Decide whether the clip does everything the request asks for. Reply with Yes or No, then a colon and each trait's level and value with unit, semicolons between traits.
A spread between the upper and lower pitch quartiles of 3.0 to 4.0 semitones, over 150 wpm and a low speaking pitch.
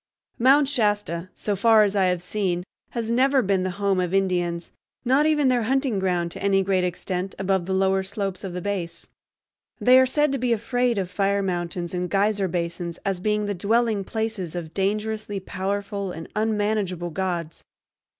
No: average, 3.3 semitones; average, 180 wpm; high, 195 Hz